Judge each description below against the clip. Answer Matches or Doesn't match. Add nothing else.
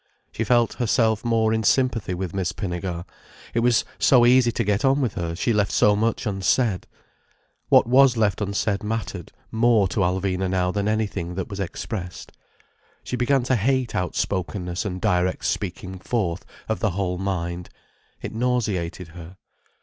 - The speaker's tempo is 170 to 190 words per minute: Doesn't match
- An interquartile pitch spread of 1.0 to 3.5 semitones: Doesn't match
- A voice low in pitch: Matches